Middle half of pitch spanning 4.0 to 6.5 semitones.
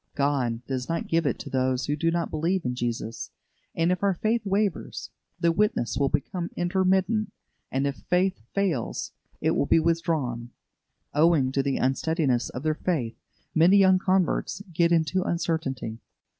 Yes: wide, 5.4 semitones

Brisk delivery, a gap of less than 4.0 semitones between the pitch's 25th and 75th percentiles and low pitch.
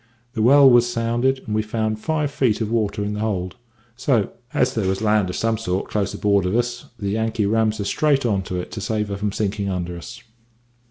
Yes: fast, 225 wpm; average, 2.9 semitones; low, 110 Hz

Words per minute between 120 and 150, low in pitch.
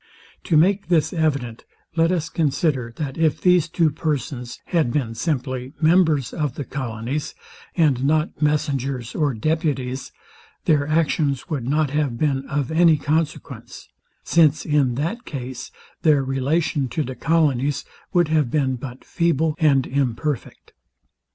No: average, 140 wpm; medium, 145 Hz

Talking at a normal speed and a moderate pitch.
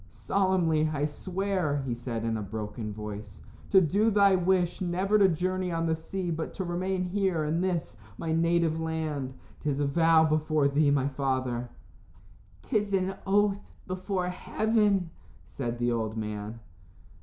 Yes: average, 155 wpm; medium, 165 Hz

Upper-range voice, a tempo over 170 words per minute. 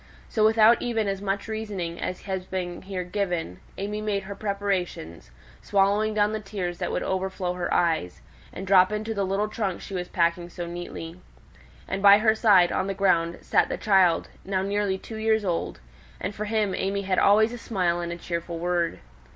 Yes: high, 195 Hz; average, 190 wpm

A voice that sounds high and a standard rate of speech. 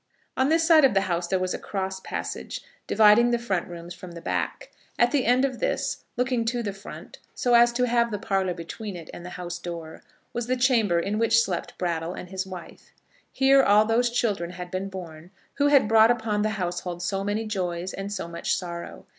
No: high, 200 Hz; fast, 215 wpm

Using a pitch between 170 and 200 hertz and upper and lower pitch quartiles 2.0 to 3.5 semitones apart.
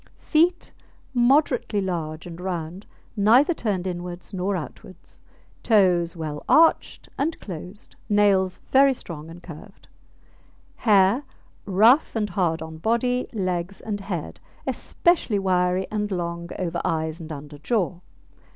No: high, 190 Hz; average, 4.1 semitones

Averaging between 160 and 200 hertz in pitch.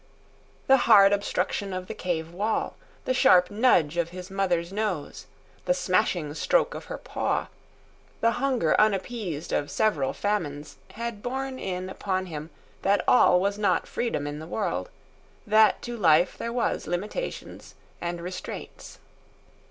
Yes: high, 190 Hz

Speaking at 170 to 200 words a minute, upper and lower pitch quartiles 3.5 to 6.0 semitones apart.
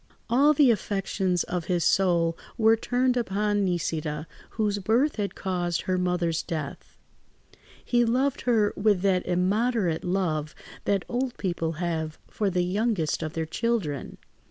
No: average, 140 wpm; average, 4.6 semitones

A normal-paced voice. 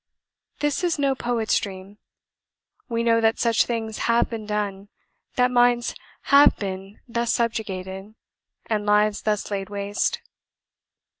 No: slow, 130 wpm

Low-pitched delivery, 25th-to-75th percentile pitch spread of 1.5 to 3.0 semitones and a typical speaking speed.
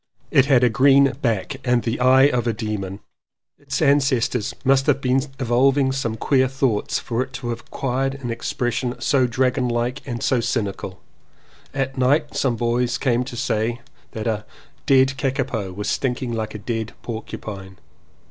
Yes: low, 125 Hz; narrow, 2.6 semitones; average, 165 wpm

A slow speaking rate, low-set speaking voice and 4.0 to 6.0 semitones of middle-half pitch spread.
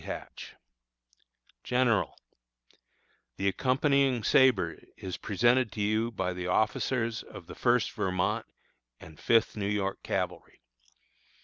Yes: slow, 110 wpm; low, 110 Hz; average, 4.4 semitones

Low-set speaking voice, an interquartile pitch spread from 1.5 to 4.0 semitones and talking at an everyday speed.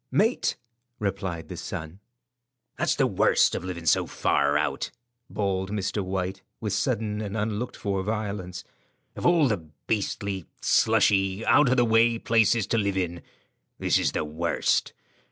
Yes: low, 100 Hz; average, 3.4 semitones; average, 150 wpm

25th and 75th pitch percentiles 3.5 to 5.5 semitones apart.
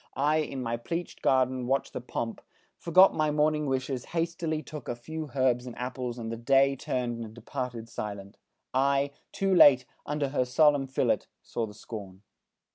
Yes: average, 3.8 semitones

